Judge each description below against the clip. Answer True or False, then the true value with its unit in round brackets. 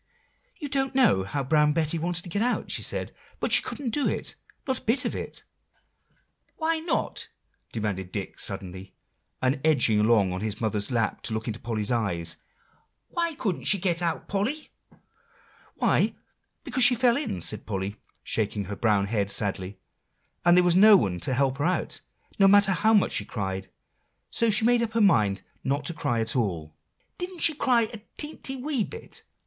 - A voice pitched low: False (150 Hz)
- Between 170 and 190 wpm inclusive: True (185 wpm)